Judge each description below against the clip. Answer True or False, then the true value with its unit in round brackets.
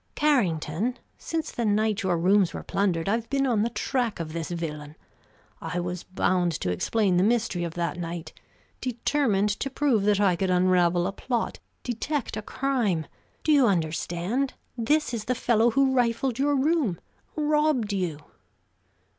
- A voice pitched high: True (210 Hz)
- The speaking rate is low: False (160 wpm)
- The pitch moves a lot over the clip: True (6.4 semitones)